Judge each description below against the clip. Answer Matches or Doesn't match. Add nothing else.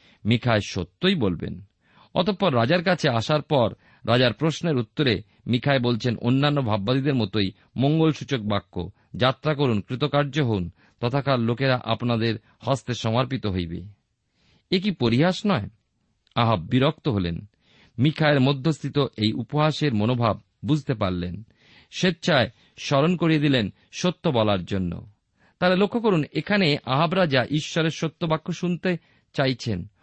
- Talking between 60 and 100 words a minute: Doesn't match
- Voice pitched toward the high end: Doesn't match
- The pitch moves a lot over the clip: Matches